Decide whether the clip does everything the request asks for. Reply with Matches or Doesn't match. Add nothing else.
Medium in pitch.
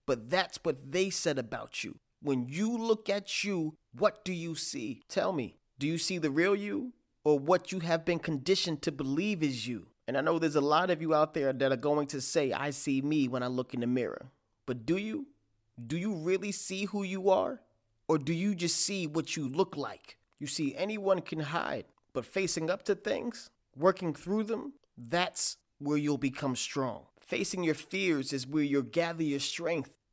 Matches